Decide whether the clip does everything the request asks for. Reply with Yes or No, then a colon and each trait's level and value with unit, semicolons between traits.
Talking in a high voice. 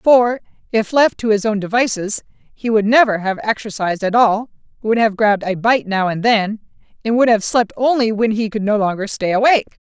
Yes: high, 220 Hz